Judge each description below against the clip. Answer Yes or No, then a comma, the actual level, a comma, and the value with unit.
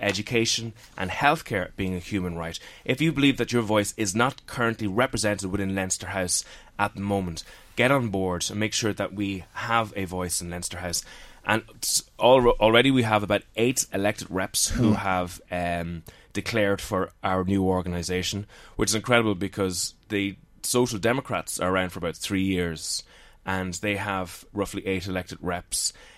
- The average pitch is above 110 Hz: No, low, 100 Hz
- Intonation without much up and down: No, average, 3.1 semitones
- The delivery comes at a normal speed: Yes, average, 170 wpm